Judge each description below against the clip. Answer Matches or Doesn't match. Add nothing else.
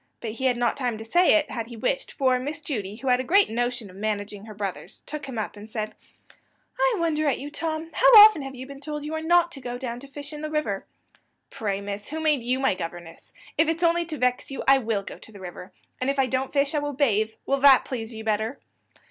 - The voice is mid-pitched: Doesn't match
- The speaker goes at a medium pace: Doesn't match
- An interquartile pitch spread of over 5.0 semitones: Matches